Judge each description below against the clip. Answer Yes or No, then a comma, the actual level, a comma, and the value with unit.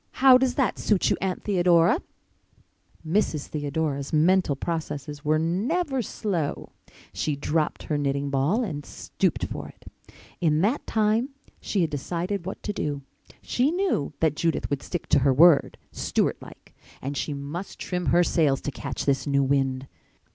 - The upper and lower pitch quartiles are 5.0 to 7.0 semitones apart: Yes, wide, 5.4 semitones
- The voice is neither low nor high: Yes, medium, 160 Hz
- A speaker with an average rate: Yes, average, 160 wpm